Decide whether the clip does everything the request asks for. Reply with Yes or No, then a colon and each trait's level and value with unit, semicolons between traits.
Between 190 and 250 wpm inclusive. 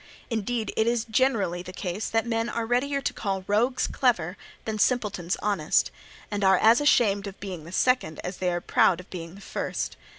Yes: average, 195 wpm